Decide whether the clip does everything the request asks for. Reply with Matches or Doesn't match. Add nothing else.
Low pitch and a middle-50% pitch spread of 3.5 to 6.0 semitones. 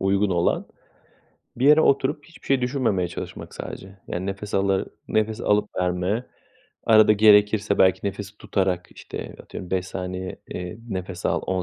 Doesn't match